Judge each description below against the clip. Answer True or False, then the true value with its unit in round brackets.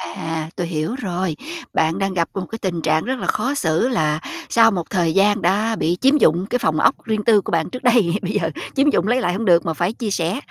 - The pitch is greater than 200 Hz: False (190 Hz)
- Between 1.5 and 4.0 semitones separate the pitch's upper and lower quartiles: False (5.2 semitones)